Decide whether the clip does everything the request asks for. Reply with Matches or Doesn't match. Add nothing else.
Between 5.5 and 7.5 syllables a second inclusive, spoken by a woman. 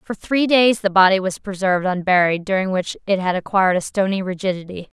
Matches